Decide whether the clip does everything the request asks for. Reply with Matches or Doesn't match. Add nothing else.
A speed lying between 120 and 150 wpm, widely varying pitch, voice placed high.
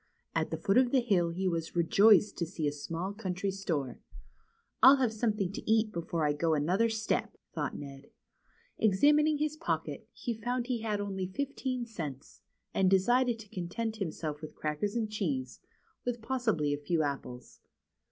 Doesn't match